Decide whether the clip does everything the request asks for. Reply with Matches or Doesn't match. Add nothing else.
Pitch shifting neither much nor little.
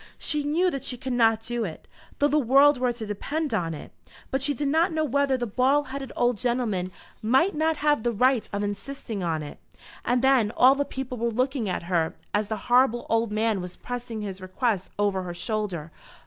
Matches